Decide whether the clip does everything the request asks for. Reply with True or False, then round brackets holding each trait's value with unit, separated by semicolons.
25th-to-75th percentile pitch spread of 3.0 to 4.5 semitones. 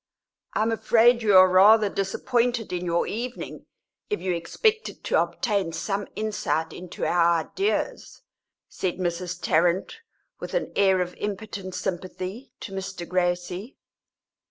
True (3.9 semitones)